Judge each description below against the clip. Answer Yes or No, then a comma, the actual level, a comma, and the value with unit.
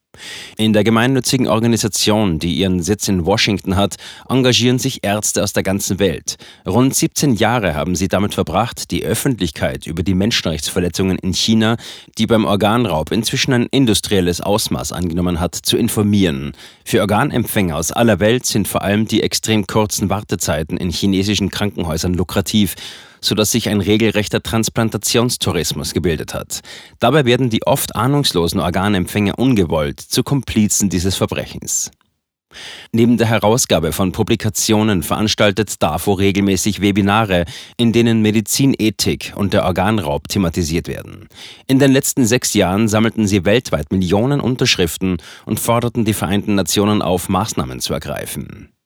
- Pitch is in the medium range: No, low, 105 Hz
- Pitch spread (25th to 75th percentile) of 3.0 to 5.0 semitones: Yes, average, 3.3 semitones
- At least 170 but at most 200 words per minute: No, average, 140 wpm